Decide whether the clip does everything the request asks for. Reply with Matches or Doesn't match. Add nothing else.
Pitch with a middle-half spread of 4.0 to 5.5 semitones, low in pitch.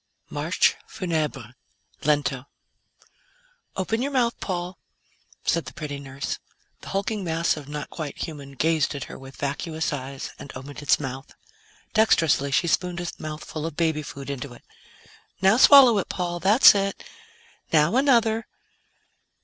Doesn't match